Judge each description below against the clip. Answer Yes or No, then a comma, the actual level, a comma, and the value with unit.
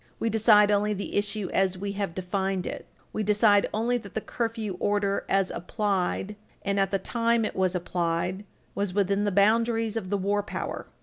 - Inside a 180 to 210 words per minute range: Yes, average, 185 wpm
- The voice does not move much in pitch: Yes, narrow, 2.0 semitones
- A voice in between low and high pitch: No, high, 205 Hz